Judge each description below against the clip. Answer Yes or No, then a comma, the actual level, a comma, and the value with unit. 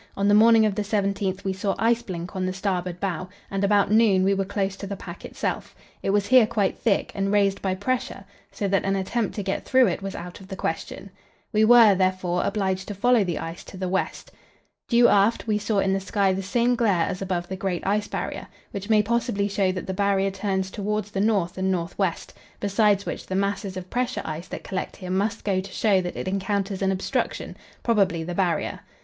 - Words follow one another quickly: Yes, fast, 225 wpm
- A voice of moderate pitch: No, high, 195 Hz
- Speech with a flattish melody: Yes, narrow, 1.9 semitones